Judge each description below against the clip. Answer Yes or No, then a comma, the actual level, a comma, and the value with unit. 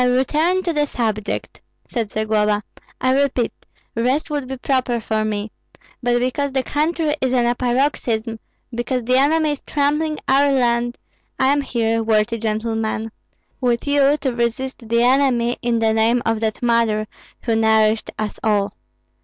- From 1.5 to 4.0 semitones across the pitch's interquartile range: Yes, average, 3.4 semitones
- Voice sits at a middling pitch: No, high, 240 Hz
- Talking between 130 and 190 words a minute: Yes, average, 160 wpm